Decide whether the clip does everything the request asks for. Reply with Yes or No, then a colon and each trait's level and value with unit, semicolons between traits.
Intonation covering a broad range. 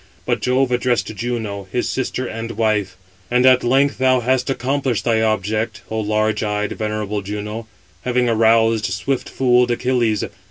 No: average, 2.8 semitones